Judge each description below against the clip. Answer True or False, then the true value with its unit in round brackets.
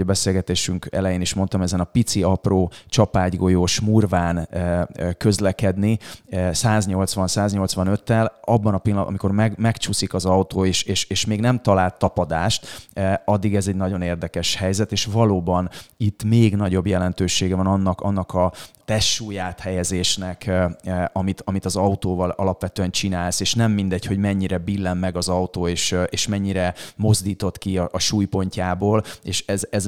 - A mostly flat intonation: True (1.9 semitones)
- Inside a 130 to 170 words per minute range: True (145 wpm)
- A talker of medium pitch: False (95 Hz)